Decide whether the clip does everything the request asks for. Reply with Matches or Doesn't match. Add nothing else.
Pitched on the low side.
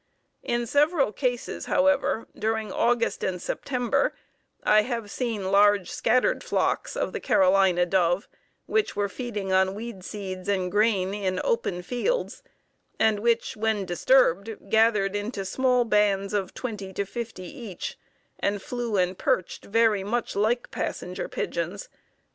Doesn't match